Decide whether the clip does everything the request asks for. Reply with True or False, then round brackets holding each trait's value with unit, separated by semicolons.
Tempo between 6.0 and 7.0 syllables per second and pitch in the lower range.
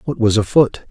False (5.1 syllables/s; 115 Hz)